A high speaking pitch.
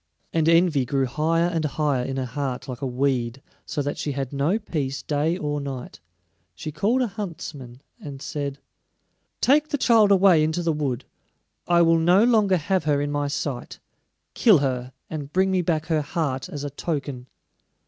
No: medium, 150 Hz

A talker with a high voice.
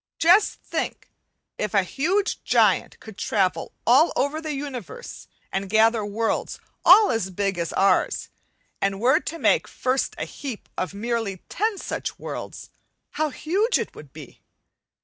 Yes: high, 235 Hz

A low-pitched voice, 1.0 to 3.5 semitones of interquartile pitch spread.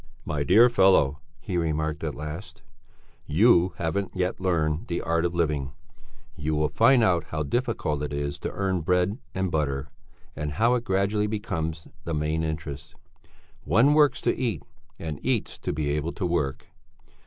No: very low, 80 Hz; average, 4.3 semitones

